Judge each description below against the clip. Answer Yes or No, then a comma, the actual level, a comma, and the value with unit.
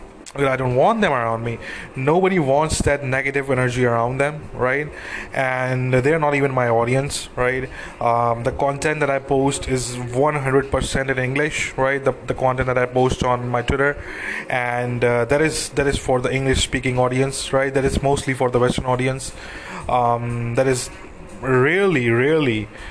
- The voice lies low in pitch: Yes, low, 130 Hz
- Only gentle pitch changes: Yes, narrow, 2.0 semitones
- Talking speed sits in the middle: Yes, average, 170 wpm